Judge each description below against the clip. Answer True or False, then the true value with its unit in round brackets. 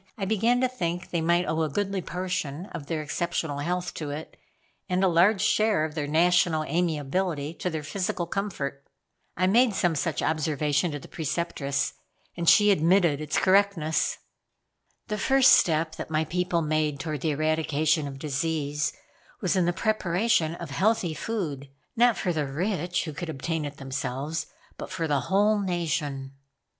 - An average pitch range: True (3.6 semitones)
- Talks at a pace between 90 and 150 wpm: False (165 wpm)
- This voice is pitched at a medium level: True (165 Hz)